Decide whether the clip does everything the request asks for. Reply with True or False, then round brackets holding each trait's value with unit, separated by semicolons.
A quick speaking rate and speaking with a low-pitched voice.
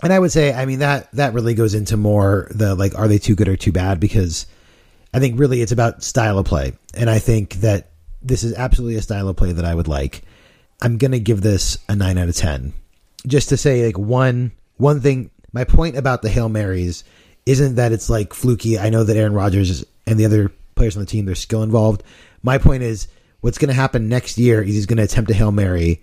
True (240 wpm; 110 Hz)